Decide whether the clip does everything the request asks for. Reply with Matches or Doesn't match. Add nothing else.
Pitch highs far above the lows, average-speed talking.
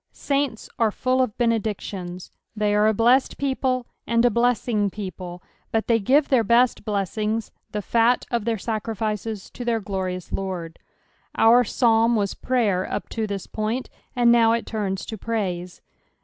Doesn't match